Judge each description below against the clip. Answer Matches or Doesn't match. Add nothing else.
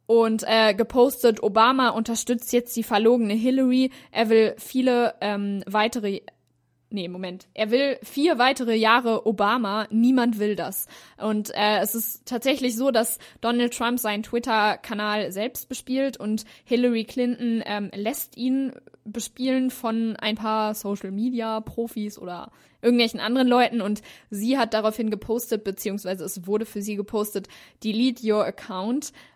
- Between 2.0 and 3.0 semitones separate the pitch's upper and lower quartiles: Matches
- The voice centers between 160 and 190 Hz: Doesn't match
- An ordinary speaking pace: Matches